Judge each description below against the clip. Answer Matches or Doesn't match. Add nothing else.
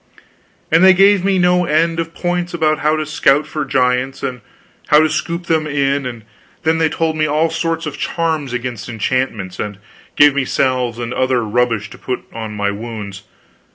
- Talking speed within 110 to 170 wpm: Doesn't match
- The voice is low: Doesn't match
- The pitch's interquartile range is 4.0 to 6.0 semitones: Matches